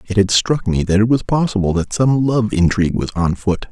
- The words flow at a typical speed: No, fast, 240 wpm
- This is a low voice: Yes, low, 105 Hz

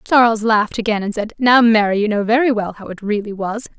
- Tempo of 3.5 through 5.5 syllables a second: No, 5.9 syllables/s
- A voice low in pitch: No, high, 220 Hz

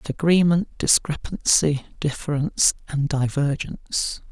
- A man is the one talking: Yes, male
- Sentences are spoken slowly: Yes, slow, 70 wpm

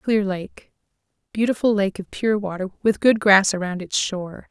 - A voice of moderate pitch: No, high, 200 Hz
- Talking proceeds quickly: No, average, 160 wpm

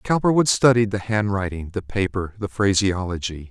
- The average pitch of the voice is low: Yes, low, 100 Hz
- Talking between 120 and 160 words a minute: Yes, slow, 135 wpm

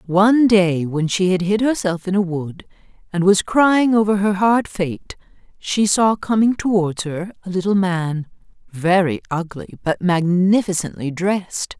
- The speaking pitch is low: No, high, 190 Hz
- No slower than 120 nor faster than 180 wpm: Yes, average, 155 wpm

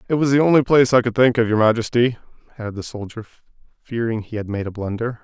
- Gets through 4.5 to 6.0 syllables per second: No, 6.9 syllables/s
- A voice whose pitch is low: Yes, low, 115 Hz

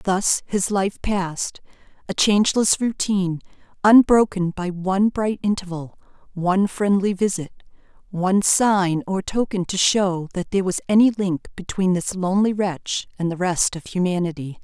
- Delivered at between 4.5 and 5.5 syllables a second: Yes, 4.7 syllables/s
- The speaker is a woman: Yes, female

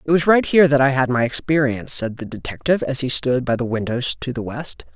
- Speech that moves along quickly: Yes, fast, 255 wpm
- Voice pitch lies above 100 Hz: Yes, low, 135 Hz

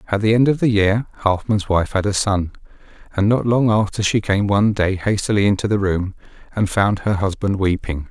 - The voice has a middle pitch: No, low, 100 Hz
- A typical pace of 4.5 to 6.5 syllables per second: Yes, 5.3 syllables/s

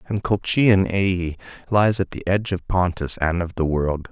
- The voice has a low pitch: Yes, very low, 90 Hz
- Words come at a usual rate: Yes, average, 190 wpm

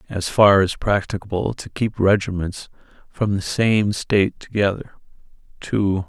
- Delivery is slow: Yes, slow, 130 wpm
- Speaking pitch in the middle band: No, low, 100 Hz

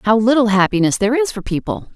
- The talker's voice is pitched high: Yes, high, 220 Hz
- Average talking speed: No, fast, 215 wpm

